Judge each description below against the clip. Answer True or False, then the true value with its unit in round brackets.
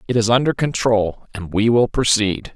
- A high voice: False (110 Hz)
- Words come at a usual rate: True (190 wpm)